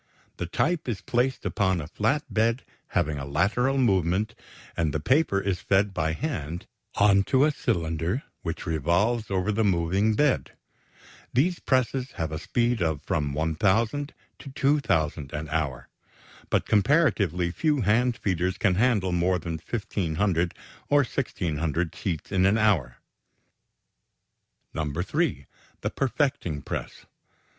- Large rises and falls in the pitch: Yes, wide, 6.7 semitones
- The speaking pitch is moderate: No, very low, 95 Hz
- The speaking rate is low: Yes, slow, 130 wpm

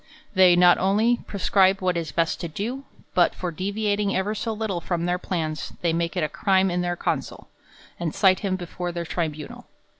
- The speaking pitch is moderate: Yes, medium, 180 Hz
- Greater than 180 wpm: Yes, average, 190 wpm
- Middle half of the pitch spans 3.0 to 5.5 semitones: No, narrow, 2.5 semitones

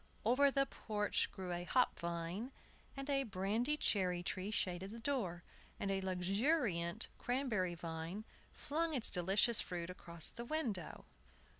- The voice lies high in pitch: Yes, high, 200 Hz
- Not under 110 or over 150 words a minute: Yes, average, 140 wpm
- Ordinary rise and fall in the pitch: No, wide, 6.0 semitones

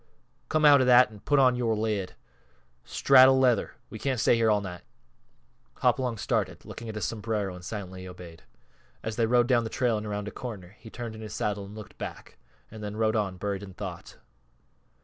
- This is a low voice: Yes, low, 110 Hz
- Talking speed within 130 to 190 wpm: No, fast, 205 wpm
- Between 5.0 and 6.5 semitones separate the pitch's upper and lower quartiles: No, average, 3.1 semitones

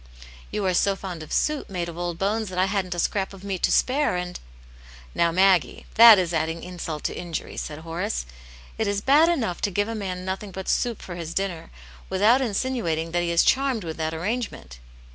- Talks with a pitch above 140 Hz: Yes, medium, 185 Hz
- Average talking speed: No, fast, 220 wpm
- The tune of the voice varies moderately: Yes, average, 3.7 semitones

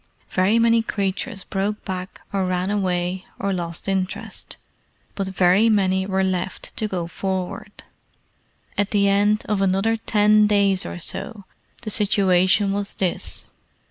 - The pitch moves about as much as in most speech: No, narrow, 1.9 semitones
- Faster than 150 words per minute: No, average, 140 wpm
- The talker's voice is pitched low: No, high, 195 Hz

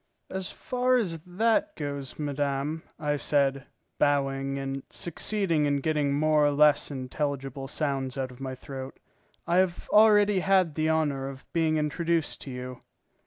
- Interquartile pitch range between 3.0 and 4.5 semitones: Yes, average, 3.4 semitones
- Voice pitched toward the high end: No, medium, 145 Hz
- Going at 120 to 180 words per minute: Yes, average, 150 wpm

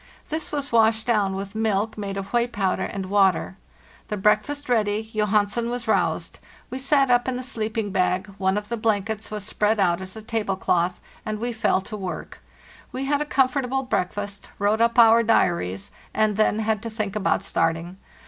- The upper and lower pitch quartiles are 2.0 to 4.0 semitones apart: Yes, average, 3.0 semitones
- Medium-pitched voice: No, high, 215 Hz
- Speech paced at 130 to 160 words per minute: No, average, 190 wpm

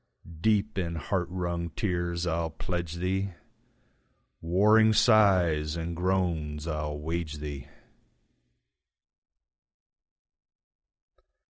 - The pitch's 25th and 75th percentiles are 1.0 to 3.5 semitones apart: Yes, average, 2.8 semitones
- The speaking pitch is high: No, very low, 85 Hz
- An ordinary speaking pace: No, slow, 75 wpm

